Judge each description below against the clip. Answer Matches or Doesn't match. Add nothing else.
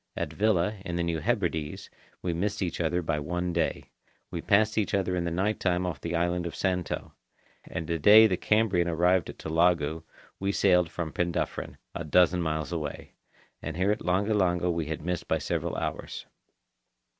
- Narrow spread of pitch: Matches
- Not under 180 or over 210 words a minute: Matches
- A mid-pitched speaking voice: Doesn't match